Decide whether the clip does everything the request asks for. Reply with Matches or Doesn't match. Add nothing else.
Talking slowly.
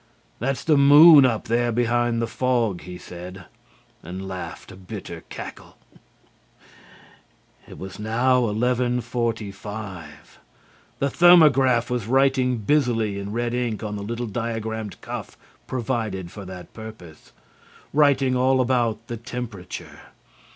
Matches